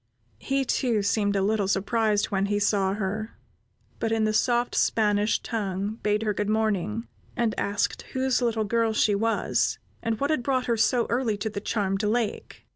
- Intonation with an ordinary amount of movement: No, narrow, 2.1 semitones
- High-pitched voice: Yes, high, 215 Hz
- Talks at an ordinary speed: Yes, average, 180 wpm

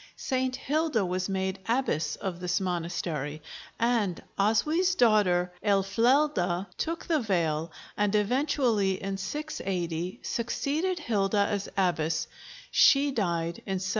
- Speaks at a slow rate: Yes, slow, 115 wpm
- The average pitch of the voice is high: Yes, high, 200 Hz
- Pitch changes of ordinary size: No, wide, 6.2 semitones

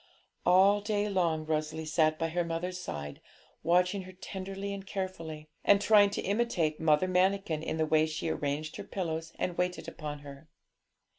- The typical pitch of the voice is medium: Yes, medium, 170 Hz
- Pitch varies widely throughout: No, average, 3.4 semitones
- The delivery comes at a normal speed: Yes, average, 165 wpm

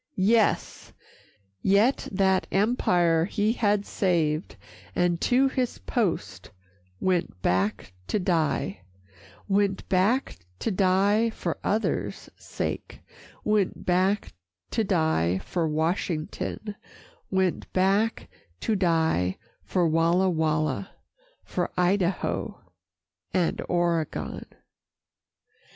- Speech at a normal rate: No, slow, 90 wpm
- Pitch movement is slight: No, average, 3.9 semitones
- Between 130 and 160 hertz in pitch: No, medium, 185 Hz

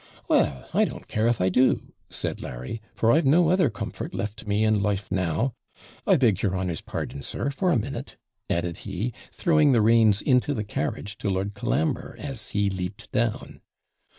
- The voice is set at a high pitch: No, low, 105 Hz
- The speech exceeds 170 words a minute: Yes, average, 180 wpm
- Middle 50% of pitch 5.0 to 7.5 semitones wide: No, average, 4.5 semitones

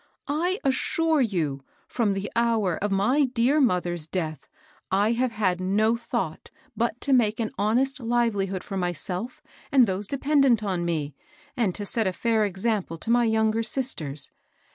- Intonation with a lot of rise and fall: No, average, 4.5 semitones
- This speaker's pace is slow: No, average, 165 wpm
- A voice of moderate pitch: No, high, 220 Hz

